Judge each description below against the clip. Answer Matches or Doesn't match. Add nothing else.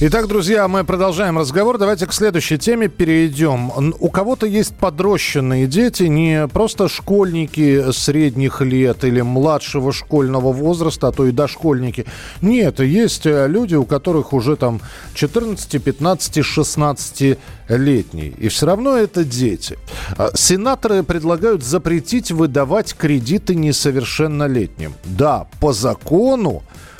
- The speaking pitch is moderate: Matches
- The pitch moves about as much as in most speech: Doesn't match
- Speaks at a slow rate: Doesn't match